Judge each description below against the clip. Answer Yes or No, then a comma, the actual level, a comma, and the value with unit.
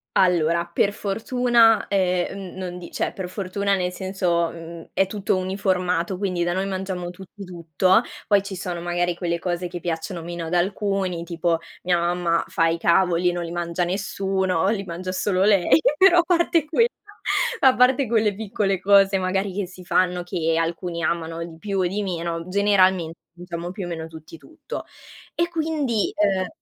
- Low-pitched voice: No, medium, 185 Hz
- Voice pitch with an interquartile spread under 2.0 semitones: No, narrow, 2.5 semitones